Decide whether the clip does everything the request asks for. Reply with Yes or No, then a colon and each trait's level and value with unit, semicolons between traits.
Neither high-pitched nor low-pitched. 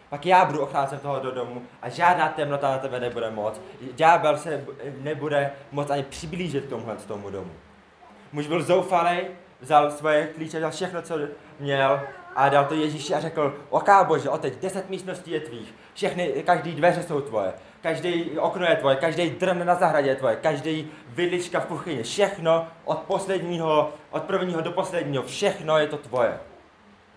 Yes: medium, 155 Hz